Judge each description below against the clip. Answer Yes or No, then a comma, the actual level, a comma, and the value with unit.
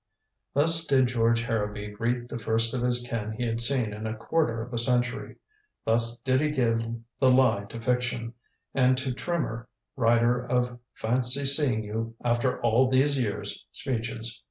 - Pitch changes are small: Yes, narrow, 2.2 semitones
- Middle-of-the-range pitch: No, low, 120 Hz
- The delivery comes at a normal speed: Yes, average, 165 wpm